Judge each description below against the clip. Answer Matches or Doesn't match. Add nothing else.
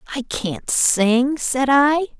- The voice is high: Matches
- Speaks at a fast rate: Doesn't match